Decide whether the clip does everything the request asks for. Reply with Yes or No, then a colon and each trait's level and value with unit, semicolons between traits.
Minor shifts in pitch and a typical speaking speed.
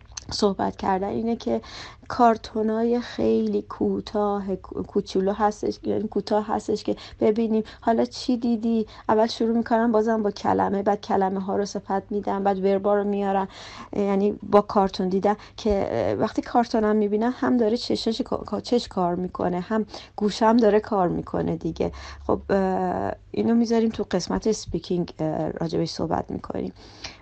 No: average, 3.1 semitones; average, 135 wpm